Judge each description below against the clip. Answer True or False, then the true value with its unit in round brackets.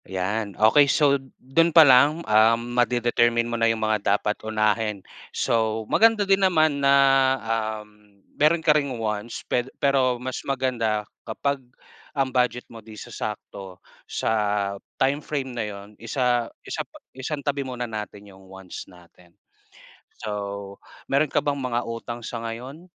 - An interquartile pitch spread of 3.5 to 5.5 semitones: True (4.3 semitones)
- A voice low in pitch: True (120 Hz)